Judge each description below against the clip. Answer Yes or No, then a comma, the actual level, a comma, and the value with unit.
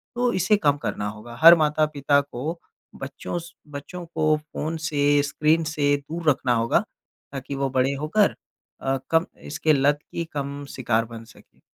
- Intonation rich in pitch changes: No, average, 3.0 semitones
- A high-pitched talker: No, medium, 145 Hz